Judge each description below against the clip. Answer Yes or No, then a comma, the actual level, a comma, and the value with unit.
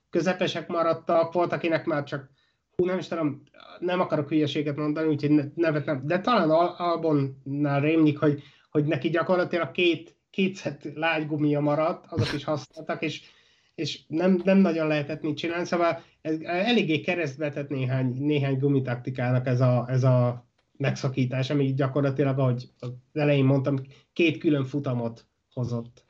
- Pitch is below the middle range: No, medium, 150 Hz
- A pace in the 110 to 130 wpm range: No, average, 145 wpm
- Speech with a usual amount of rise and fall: Yes, average, 3.2 semitones